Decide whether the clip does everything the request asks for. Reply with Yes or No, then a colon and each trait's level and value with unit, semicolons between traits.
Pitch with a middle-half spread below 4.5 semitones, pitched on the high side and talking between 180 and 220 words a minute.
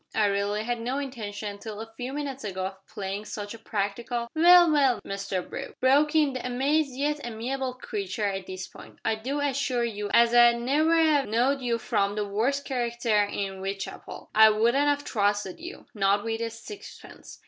No: average, 4.9 semitones; high, 235 Hz; average, 190 wpm